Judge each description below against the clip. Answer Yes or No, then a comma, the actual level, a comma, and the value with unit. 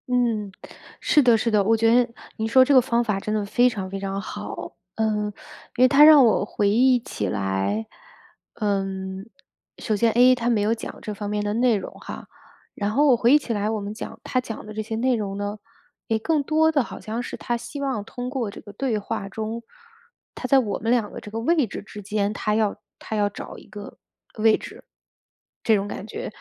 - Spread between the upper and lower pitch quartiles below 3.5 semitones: Yes, average, 3.1 semitones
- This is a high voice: Yes, high, 220 Hz